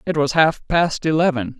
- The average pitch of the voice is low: No, medium, 155 Hz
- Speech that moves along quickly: No, average, 190 wpm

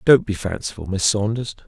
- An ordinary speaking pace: Yes, average, 180 wpm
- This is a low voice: Yes, low, 105 Hz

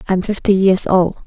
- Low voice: No, high, 190 Hz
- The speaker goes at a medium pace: Yes, average, 190 wpm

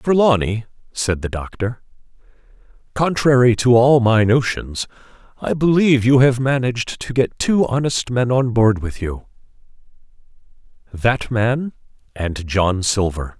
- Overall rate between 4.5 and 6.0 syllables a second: No, 4.3 syllables/s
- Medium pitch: No, low, 120 Hz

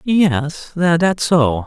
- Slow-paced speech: Yes, slow, 110 wpm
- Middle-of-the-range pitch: Yes, medium, 160 Hz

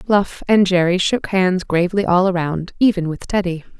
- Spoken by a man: No, female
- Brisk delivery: No, average, 175 wpm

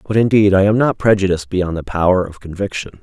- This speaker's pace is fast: Yes, fast, 220 wpm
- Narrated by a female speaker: No, male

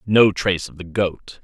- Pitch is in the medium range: No, very low, 95 Hz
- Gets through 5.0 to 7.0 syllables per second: No, 4.5 syllables/s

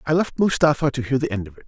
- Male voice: Yes, male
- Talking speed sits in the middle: No, fast, 320 wpm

